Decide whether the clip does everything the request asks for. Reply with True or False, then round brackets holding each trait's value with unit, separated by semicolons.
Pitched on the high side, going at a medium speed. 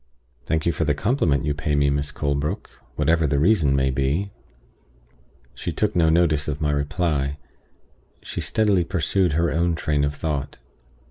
False (75 Hz; 160 wpm)